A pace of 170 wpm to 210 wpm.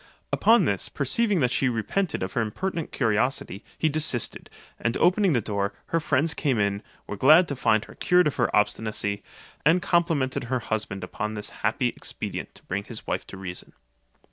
Yes: average, 180 wpm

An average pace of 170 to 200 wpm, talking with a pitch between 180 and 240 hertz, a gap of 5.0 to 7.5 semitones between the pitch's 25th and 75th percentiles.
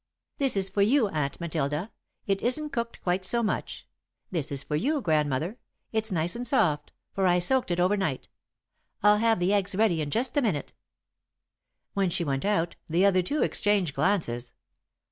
Yes: average, 180 wpm; high, 190 Hz; wide, 5.6 semitones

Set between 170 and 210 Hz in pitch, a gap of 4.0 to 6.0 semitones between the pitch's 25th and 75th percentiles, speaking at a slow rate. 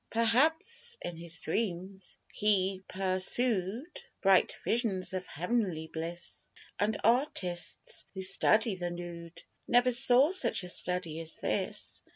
Yes: high, 190 Hz; average, 5.1 semitones; slow, 120 wpm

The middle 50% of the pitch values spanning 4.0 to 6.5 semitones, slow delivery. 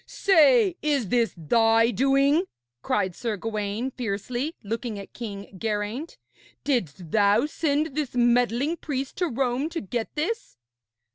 Yes: wide, 5.6 semitones; slow, 130 wpm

